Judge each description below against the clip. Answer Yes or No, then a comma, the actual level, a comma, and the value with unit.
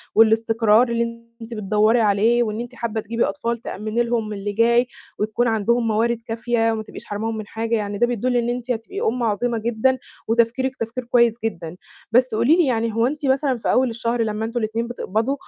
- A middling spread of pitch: No, narrow, 1.6 semitones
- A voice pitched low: No, high, 230 Hz